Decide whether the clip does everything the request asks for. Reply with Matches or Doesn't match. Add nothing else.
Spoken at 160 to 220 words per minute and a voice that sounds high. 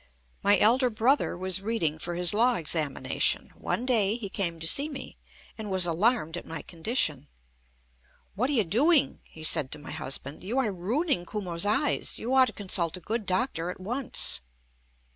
Matches